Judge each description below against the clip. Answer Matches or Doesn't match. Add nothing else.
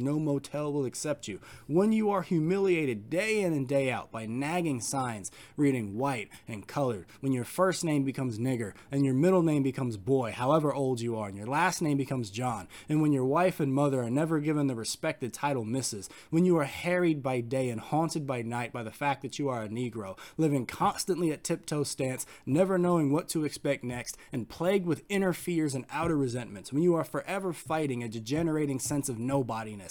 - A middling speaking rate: Doesn't match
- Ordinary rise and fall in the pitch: Matches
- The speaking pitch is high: Doesn't match